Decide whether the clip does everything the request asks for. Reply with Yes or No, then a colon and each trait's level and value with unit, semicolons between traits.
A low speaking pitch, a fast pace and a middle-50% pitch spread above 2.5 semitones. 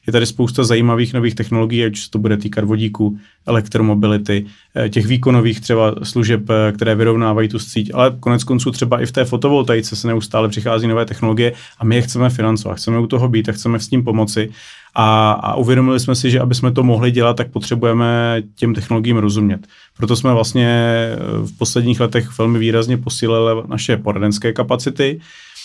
No: low, 115 Hz; fast, 180 wpm; narrow, 1.9 semitones